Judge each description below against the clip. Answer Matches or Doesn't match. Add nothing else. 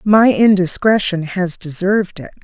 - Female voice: Matches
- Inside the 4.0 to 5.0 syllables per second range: Matches